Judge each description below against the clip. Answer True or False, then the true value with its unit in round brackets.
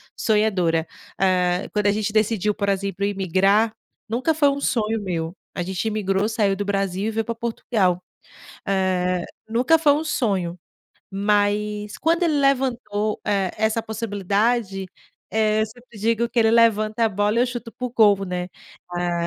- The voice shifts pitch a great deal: False (3.0 semitones)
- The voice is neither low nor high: False (210 Hz)